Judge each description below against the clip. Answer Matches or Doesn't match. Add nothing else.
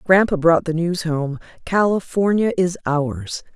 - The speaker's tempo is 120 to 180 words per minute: Matches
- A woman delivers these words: Matches